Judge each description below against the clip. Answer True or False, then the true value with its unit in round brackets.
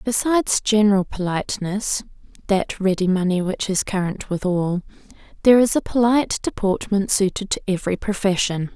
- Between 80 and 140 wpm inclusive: True (135 wpm)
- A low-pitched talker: False (200 Hz)